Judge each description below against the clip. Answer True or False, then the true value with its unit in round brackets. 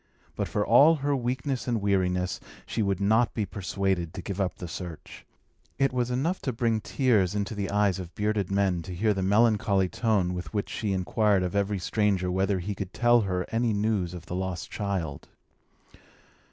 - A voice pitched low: True (100 Hz)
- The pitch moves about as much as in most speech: True (3.4 semitones)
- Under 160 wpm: False (190 wpm)